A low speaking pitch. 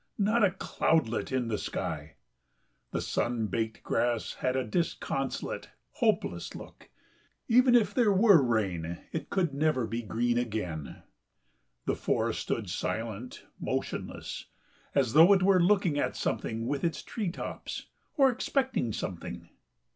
Yes: low, 130 Hz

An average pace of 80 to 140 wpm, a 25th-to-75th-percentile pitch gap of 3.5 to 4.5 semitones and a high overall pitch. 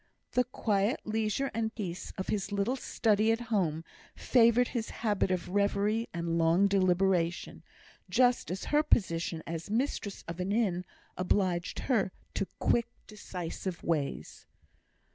Yes: slow, 135 wpm; average, 4.2 semitones; high, 200 Hz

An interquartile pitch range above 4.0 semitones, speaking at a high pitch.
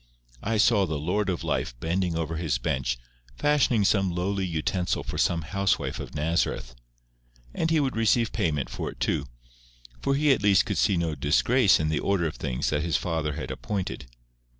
No: average, 4.9 semitones; very low, 90 Hz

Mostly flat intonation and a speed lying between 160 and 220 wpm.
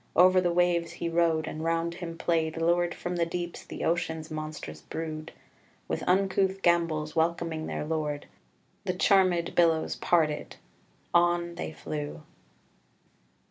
No: narrow, 1.6 semitones; slow, 135 wpm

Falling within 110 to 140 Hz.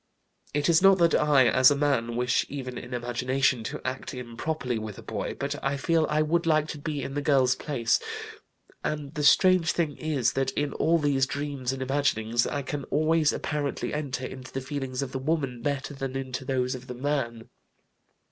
Yes: low, 135 Hz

